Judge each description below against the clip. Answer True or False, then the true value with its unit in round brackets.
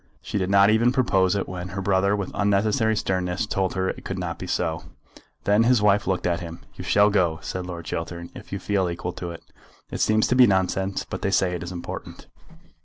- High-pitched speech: False (95 Hz)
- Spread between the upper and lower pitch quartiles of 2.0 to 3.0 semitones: True (2.4 semitones)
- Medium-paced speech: False (230 wpm)